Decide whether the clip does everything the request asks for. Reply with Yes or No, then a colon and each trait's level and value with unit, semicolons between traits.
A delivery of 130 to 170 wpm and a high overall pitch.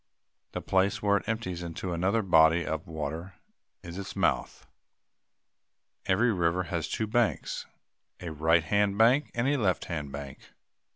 No: average, 150 wpm; very low, 90 Hz